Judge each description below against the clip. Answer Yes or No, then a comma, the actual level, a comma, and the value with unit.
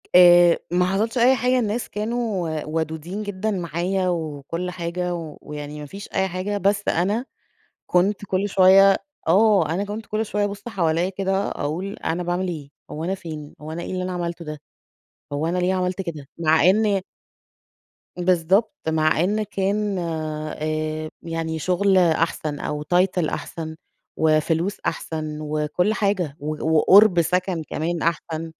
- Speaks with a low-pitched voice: No, medium, 180 Hz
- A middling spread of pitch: Yes, average, 3.6 semitones